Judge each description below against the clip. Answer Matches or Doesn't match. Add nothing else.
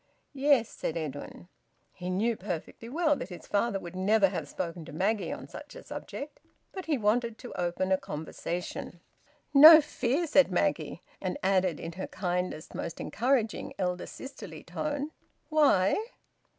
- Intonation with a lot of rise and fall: Matches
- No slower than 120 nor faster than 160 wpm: Matches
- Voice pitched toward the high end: Matches